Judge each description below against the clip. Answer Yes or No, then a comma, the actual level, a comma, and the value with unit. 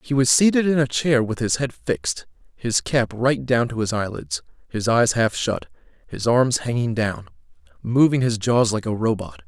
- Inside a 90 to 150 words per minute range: No, average, 195 wpm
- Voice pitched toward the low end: Yes, low, 115 Hz